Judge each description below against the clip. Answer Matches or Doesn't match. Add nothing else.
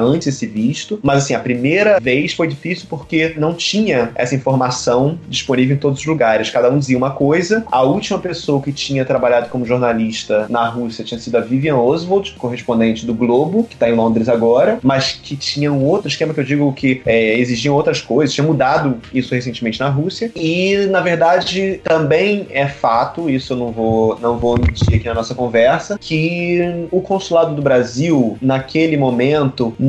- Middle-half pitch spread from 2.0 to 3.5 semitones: Doesn't match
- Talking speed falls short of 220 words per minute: Matches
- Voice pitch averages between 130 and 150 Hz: Matches